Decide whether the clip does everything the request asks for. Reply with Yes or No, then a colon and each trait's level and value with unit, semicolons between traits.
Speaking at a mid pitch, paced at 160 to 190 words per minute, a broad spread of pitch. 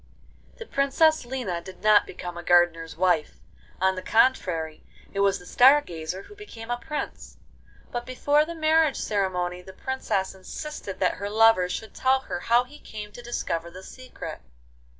No: high, 210 Hz; average, 170 wpm; wide, 6.5 semitones